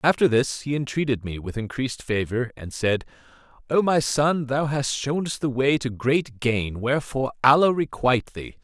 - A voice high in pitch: No, low, 130 Hz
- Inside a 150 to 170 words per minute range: No, average, 180 wpm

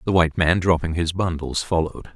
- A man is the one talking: Yes, male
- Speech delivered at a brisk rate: No, average, 195 wpm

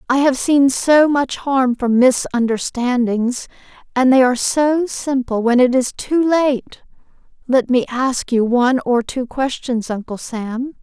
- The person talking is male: No, female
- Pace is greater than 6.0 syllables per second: No, 3.9 syllables/s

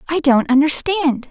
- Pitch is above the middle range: Yes, very high, 295 Hz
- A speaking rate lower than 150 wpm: Yes, average, 140 wpm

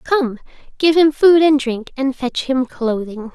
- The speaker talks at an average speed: Yes, average, 180 wpm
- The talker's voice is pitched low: No, very high, 270 Hz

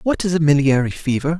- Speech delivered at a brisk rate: Yes, fast, 215 wpm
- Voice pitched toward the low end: No, medium, 155 Hz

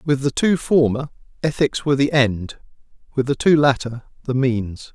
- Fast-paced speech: No, average, 170 wpm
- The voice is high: No, low, 135 Hz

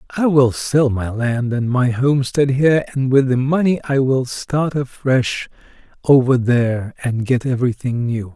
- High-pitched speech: No, low, 130 Hz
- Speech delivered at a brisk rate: No, average, 165 wpm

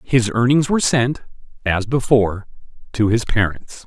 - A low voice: Yes, low, 120 Hz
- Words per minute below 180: Yes, average, 140 wpm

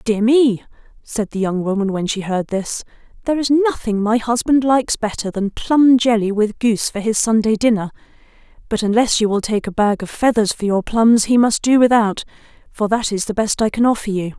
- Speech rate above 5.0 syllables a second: Yes, 5.3 syllables/s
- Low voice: No, high, 220 Hz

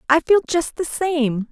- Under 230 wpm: Yes, average, 200 wpm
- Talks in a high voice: Yes, very high, 305 Hz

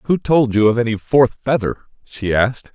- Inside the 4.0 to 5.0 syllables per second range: Yes, 4.9 syllables/s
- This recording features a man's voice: Yes, male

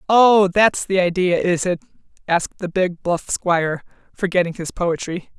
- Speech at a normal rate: Yes, average, 165 wpm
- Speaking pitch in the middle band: Yes, medium, 180 Hz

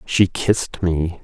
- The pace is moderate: Yes, average, 145 wpm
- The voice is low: Yes, very low, 90 Hz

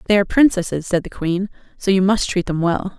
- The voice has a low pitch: No, high, 190 Hz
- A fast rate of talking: Yes, fast, 240 wpm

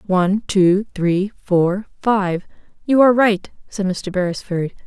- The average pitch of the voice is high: Yes, high, 195 Hz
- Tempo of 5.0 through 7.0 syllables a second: No, 4.0 syllables/s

